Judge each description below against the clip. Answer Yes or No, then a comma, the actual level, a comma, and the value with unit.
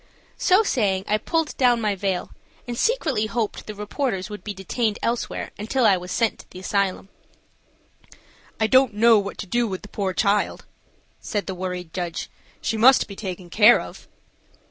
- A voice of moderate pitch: No, high, 210 Hz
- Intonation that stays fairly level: No, average, 3.6 semitones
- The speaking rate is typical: Yes, average, 175 wpm